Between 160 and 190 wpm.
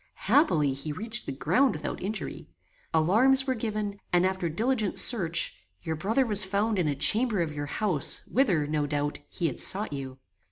Yes: average, 175 wpm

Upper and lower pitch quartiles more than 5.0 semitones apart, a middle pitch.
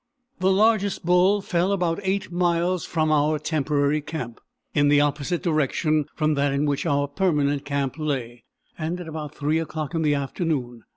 No: average, 3.4 semitones; medium, 155 Hz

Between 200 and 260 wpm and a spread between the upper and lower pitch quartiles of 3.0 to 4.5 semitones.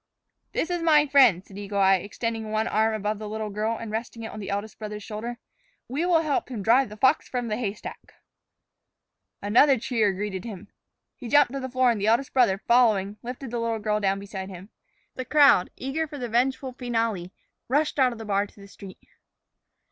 Yes: fast, 205 wpm; average, 3.8 semitones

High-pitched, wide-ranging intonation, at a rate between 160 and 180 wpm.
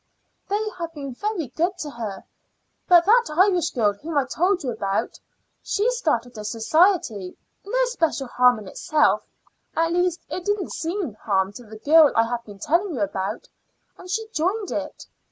Yes: very high, 315 Hz; wide, 8.3 semitones; average, 170 wpm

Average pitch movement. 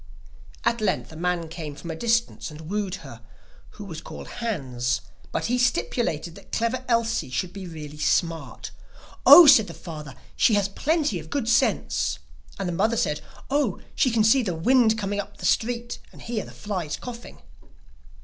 No: wide, 6.2 semitones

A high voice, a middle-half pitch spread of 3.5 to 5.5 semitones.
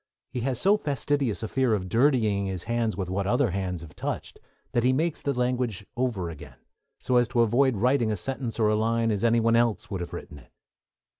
No: low, 115 Hz; average, 4.0 semitones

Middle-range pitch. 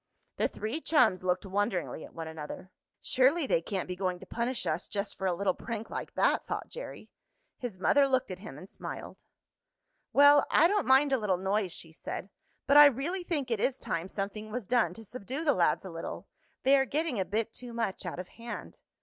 No: high, 220 Hz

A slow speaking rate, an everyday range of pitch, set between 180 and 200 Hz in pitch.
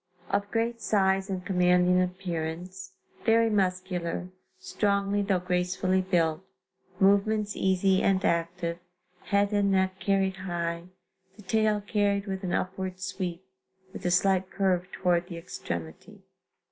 No: slow, 125 wpm; narrow, 1.9 semitones; high, 190 Hz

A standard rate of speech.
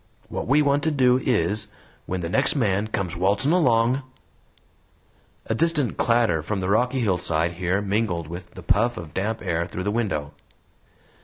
Yes: average, 170 wpm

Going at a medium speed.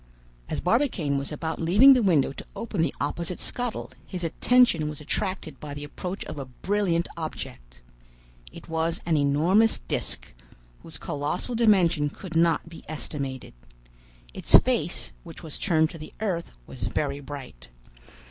Yes: average, 150 wpm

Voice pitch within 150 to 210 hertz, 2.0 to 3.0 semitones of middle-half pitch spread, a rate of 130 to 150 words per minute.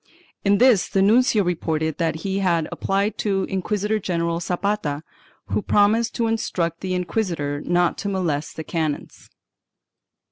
No: medium, 185 Hz; average, 3.6 semitones; average, 140 wpm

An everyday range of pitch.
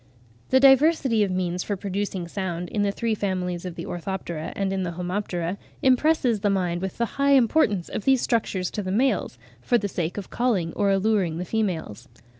Yes: average, 4.1 semitones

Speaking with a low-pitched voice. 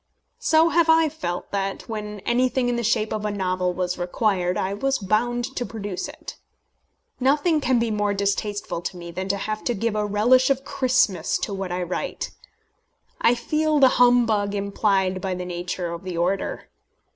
No: high, 210 Hz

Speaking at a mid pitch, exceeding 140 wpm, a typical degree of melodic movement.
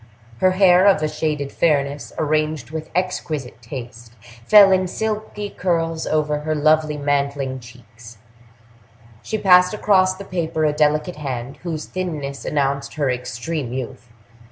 No: medium, 150 Hz; slow, 135 wpm; average, 4.6 semitones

